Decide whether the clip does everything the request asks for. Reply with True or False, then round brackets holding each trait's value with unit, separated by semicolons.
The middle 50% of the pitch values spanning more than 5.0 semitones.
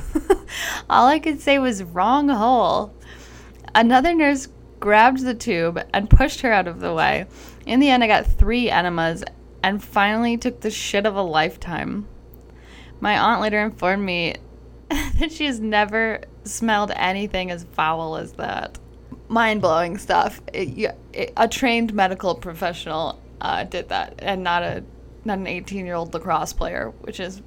True (5.4 semitones)